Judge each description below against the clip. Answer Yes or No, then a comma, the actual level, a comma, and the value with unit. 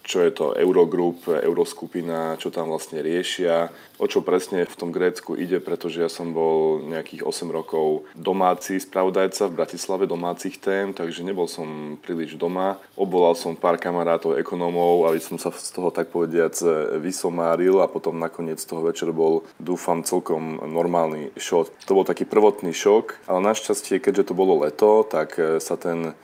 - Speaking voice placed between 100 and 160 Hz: No, very low, 85 Hz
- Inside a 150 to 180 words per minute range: Yes, average, 160 wpm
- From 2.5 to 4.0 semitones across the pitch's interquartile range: Yes, average, 2.9 semitones